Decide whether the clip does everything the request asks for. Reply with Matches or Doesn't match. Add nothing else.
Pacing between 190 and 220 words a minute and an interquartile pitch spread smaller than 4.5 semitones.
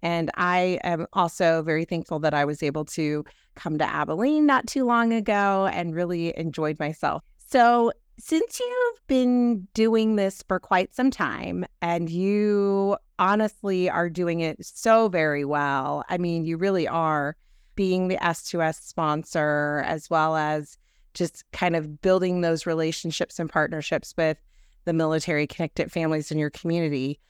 Doesn't match